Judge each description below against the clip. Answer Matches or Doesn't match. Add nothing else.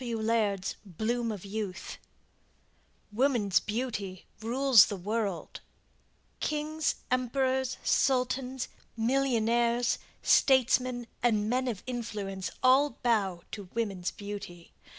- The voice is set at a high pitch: Matches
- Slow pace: Matches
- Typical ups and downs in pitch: Matches